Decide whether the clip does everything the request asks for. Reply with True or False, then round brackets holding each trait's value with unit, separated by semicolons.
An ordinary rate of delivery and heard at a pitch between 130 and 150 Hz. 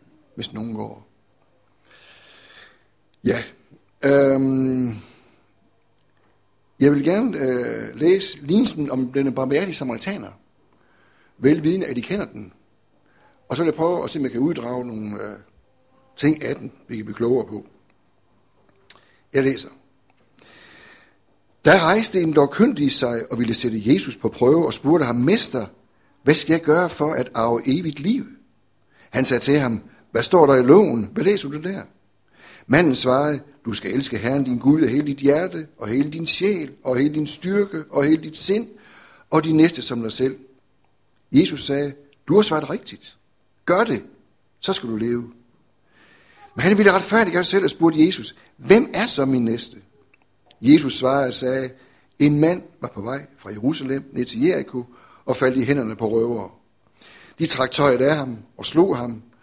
True (170 wpm; 135 Hz)